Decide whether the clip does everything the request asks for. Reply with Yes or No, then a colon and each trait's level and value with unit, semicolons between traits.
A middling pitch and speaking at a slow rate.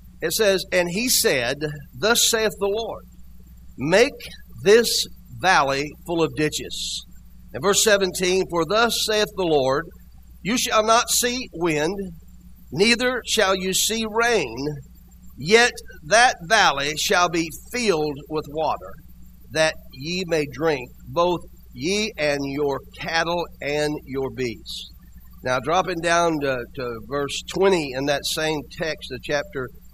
Yes: medium, 160 Hz; slow, 130 wpm